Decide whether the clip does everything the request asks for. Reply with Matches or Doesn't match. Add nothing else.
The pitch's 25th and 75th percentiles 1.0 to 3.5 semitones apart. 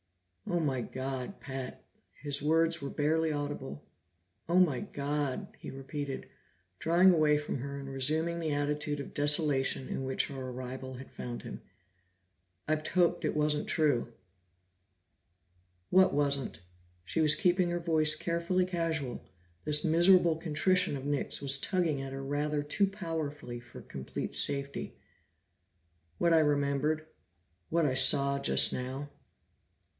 Matches